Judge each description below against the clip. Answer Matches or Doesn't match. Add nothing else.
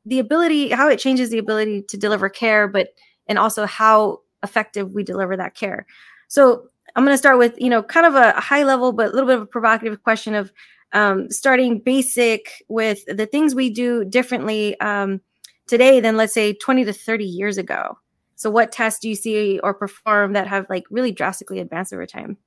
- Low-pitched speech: Doesn't match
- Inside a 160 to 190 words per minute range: Doesn't match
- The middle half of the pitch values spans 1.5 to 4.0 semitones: Matches